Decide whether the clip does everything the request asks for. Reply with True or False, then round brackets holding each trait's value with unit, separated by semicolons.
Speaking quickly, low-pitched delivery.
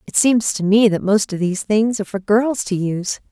False (255 wpm; 210 Hz)